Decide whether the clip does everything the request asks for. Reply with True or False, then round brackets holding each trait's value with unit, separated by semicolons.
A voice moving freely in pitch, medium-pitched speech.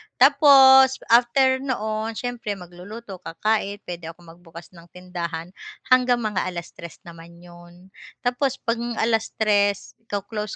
False (5.7 semitones; 205 Hz)